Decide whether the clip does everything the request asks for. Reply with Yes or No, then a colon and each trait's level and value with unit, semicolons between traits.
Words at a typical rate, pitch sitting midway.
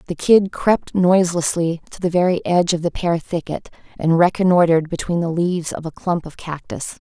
Yes: average, 185 wpm; medium, 170 Hz